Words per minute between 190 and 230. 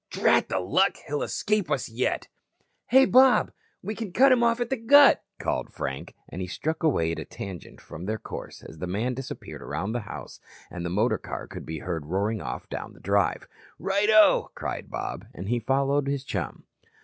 Yes: average, 195 wpm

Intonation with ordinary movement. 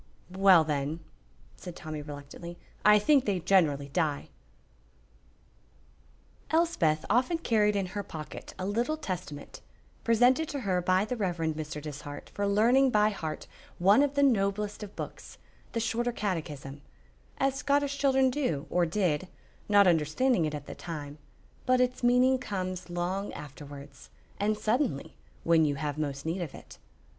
No: wide, 7.4 semitones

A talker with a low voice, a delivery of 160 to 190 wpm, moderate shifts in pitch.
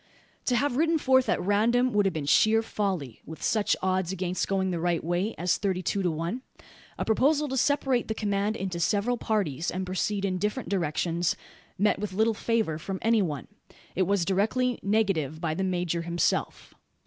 No: high, 195 Hz; average, 185 wpm; average, 4.1 semitones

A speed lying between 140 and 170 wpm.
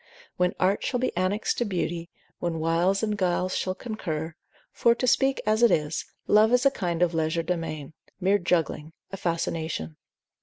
Yes: average, 165 wpm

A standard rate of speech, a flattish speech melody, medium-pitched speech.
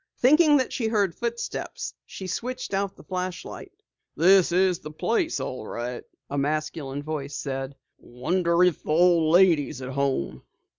No: average, 155 wpm; average, 5.3 semitones; medium, 170 Hz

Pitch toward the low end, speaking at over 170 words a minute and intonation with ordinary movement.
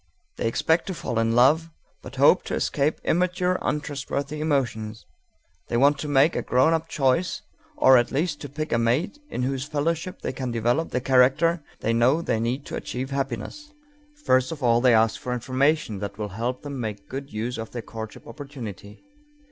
Yes: low, 130 Hz; average, 190 wpm; average, 4.5 semitones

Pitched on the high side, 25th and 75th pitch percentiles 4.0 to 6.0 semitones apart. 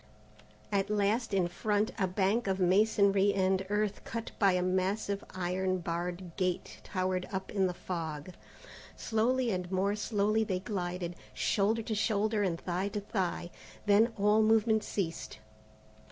No: high, 195 Hz; narrow, 2.5 semitones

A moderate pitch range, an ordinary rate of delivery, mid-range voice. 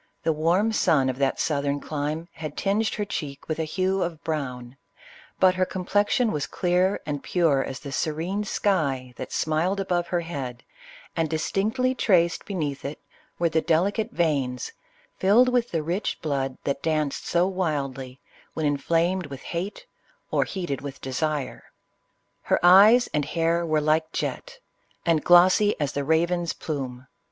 Yes: average, 4.5 semitones; average, 155 wpm; medium, 160 Hz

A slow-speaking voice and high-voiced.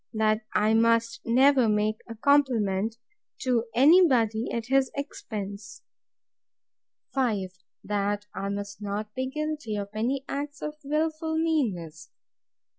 Yes: slow, 120 wpm; high, 230 Hz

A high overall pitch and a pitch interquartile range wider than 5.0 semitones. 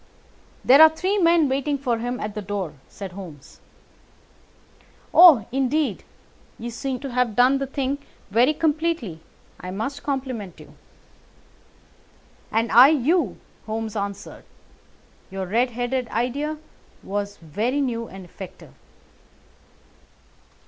Yes: high, 245 Hz; wide, 5.4 semitones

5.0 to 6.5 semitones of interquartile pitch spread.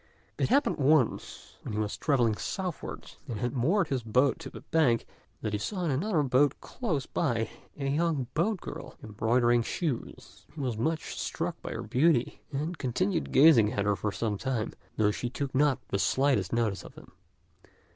Yes: wide, 5.6 semitones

